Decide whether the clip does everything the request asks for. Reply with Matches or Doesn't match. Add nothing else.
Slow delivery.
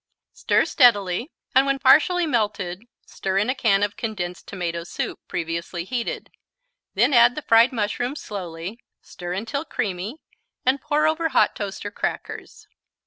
Doesn't match